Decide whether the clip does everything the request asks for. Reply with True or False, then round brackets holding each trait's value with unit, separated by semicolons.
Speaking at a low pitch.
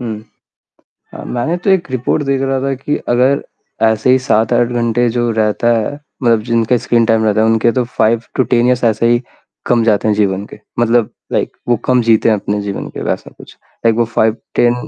True (120 Hz)